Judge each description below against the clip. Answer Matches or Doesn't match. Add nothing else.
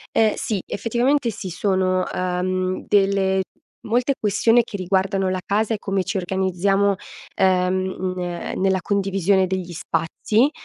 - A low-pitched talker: Doesn't match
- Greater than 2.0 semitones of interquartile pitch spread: Doesn't match